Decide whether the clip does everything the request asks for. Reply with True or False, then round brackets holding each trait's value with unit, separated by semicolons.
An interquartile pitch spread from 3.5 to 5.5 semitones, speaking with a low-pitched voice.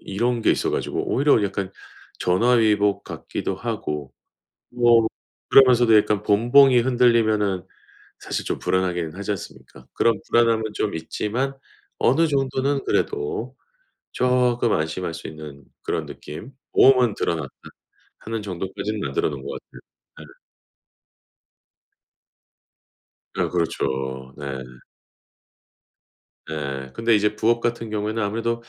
True (5.2 semitones; 110 Hz)